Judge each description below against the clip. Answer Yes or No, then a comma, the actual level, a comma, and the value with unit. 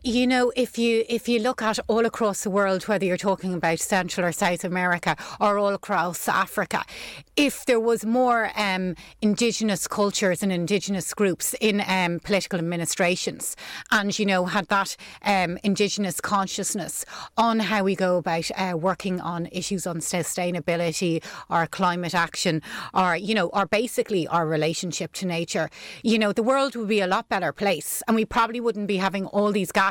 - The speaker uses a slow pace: No, average, 175 wpm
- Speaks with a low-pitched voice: No, high, 195 Hz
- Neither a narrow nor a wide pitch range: Yes, average, 3.5 semitones